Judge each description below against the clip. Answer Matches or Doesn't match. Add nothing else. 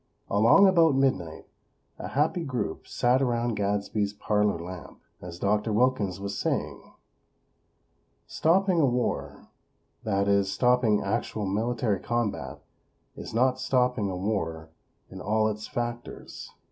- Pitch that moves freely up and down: Doesn't match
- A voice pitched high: Doesn't match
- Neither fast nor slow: Doesn't match